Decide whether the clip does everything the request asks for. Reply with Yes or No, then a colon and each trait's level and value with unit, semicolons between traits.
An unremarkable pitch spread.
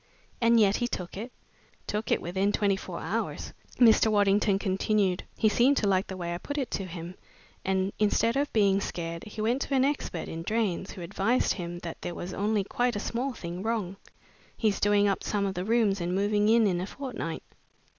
Yes: average, 3.3 semitones